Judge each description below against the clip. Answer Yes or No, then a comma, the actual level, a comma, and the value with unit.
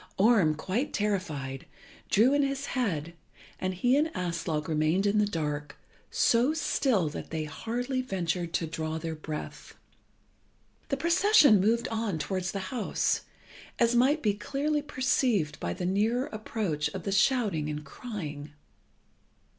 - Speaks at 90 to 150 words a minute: Yes, average, 140 wpm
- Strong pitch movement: Yes, wide, 7.5 semitones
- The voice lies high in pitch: Yes, high, 200 Hz